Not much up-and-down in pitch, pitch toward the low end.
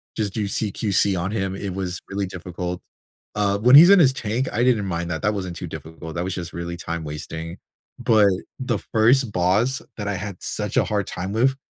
No: average, 4.0 semitones; low, 100 Hz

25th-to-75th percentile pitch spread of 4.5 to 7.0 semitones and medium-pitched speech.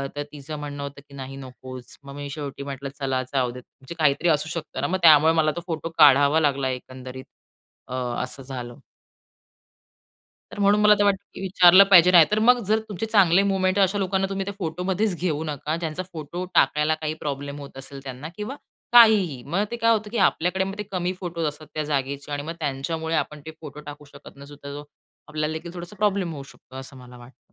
Yes: average, 4.9 semitones; medium, 155 Hz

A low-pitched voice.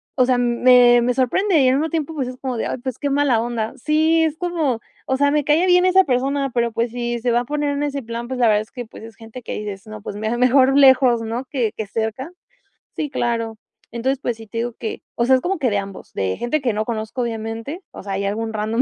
No: high, 245 Hz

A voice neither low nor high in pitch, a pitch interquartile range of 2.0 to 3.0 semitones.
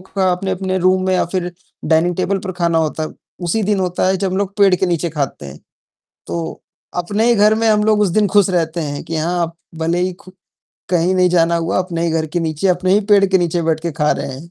Yes: medium, 180 Hz; narrow, 2.4 semitones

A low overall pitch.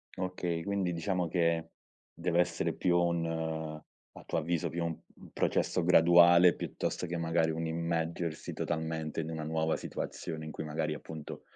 Yes: very low, 85 Hz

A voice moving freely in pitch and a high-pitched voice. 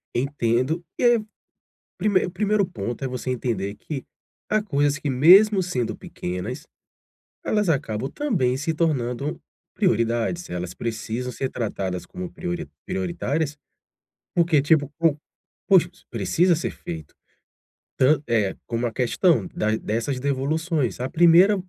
No: wide, 6.6 semitones; medium, 140 Hz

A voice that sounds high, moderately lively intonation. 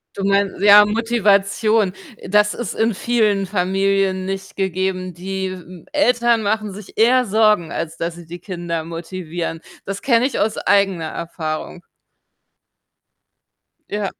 Yes: high, 195 Hz; average, 3.0 semitones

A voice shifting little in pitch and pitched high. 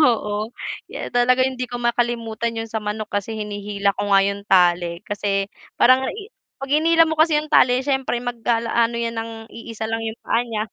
No: average, 3.2 semitones; high, 230 Hz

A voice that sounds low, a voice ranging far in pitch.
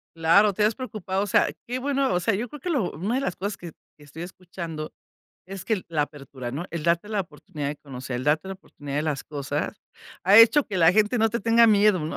No: medium, 185 Hz; wide, 5.9 semitones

